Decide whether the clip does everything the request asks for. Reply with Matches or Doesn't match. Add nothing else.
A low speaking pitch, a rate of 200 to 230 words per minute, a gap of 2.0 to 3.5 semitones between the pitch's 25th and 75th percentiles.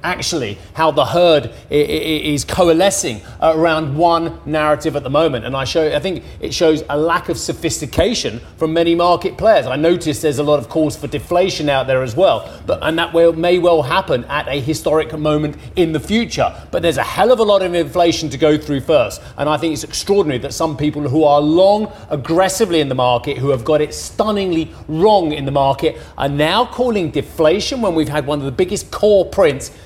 Doesn't match